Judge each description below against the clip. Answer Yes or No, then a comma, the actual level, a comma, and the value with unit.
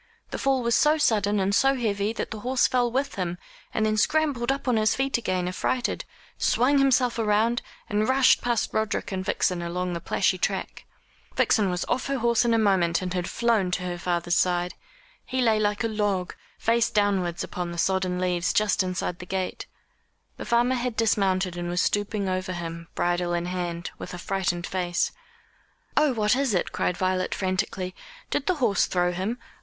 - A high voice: Yes, high, 200 Hz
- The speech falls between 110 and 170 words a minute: No, average, 190 wpm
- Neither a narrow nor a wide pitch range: Yes, average, 4.7 semitones